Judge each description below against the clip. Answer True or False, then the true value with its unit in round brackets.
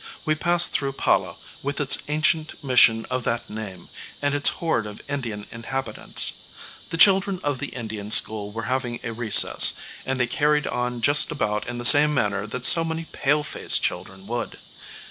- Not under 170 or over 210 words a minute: True (175 wpm)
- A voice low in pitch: True (125 Hz)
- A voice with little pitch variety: False (4.9 semitones)